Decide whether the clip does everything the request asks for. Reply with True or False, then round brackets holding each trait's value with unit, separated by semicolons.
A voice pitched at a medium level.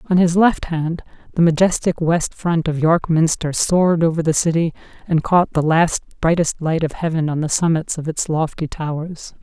True (165 Hz)